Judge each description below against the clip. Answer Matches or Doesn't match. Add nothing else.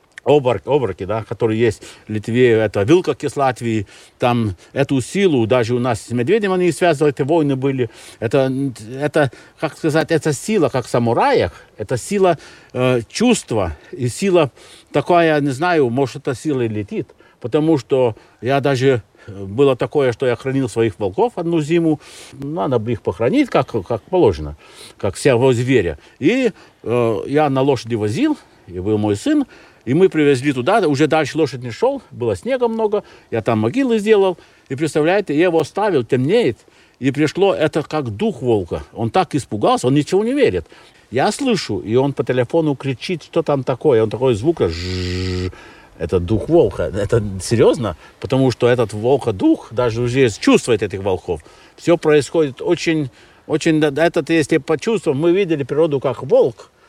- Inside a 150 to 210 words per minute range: Matches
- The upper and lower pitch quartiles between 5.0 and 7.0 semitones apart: Matches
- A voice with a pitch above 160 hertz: Doesn't match